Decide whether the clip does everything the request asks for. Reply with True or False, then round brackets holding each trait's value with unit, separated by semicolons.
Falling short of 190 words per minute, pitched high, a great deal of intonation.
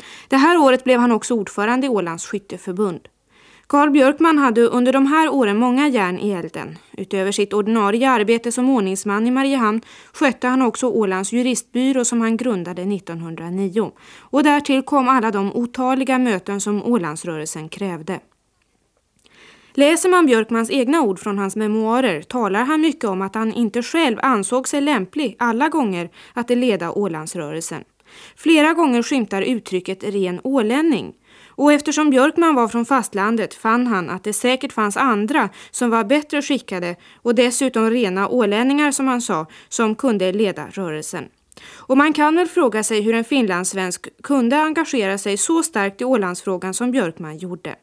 False (160 wpm; 235 Hz; 5.0 semitones)